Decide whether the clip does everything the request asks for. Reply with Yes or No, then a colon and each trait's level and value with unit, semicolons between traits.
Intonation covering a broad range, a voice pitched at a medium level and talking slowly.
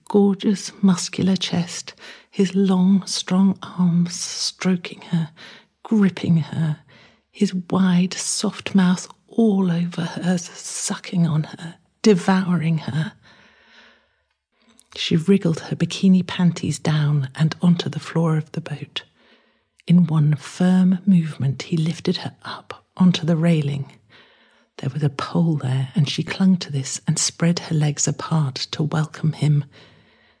No: average, 3.3 semitones; medium, 170 Hz; slow, 130 wpm